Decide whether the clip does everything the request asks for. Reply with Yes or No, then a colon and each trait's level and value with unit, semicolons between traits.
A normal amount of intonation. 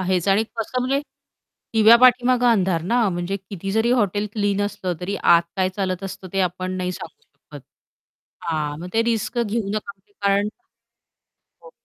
Yes: average, 3.6 semitones